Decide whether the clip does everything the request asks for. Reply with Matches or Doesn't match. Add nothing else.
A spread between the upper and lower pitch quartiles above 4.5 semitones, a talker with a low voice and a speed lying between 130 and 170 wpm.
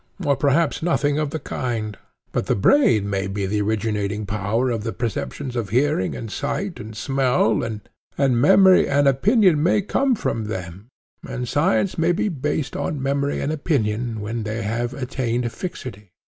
Matches